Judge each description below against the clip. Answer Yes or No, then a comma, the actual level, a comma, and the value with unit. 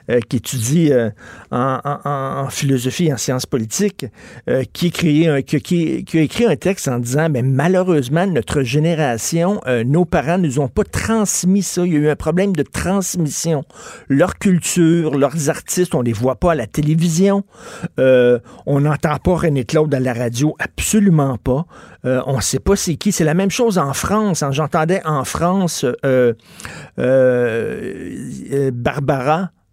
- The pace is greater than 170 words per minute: Yes, average, 180 wpm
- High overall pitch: No, medium, 155 Hz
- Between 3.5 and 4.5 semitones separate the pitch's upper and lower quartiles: No, average, 4.9 semitones